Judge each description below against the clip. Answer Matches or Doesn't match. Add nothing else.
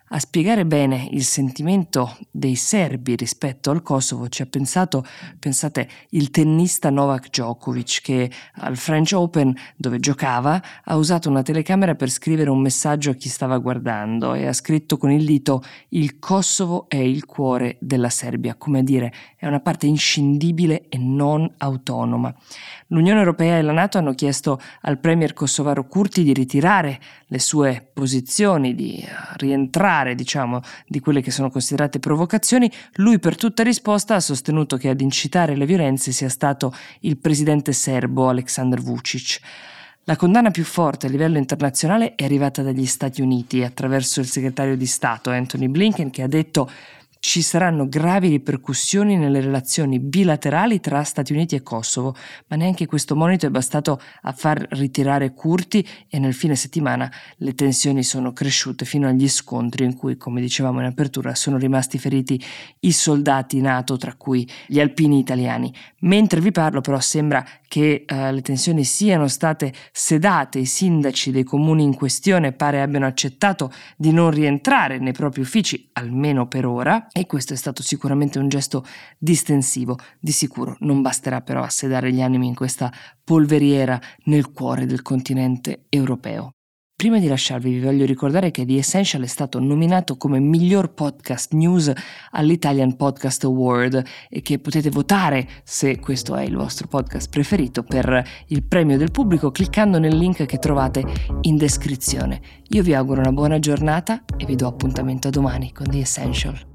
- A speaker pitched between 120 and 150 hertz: Matches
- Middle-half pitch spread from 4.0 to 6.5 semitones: Doesn't match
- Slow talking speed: Doesn't match